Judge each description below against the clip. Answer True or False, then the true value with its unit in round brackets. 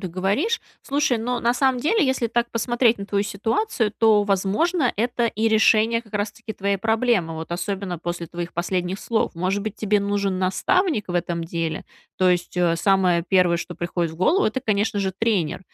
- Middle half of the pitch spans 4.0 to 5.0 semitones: True (4.3 semitones)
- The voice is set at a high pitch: True (205 Hz)